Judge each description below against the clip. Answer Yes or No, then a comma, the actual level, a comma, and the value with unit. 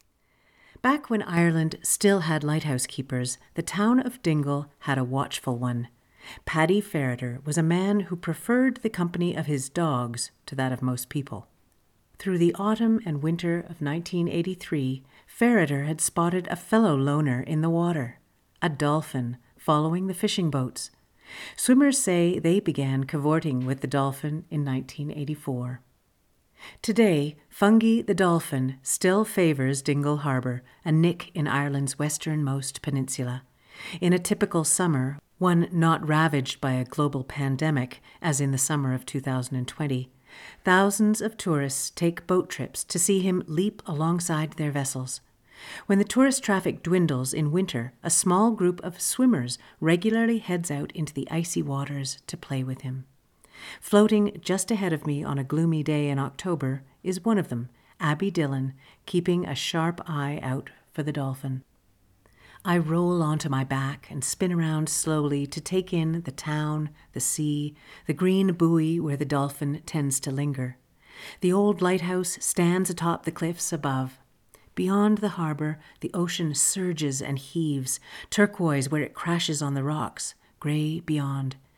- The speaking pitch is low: No, medium, 155 Hz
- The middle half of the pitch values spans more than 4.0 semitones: Yes, average, 4.7 semitones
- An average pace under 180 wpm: Yes, average, 150 wpm